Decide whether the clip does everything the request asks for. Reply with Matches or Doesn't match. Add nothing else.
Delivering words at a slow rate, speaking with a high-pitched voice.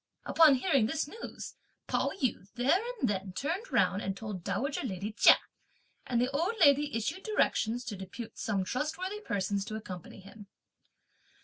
Doesn't match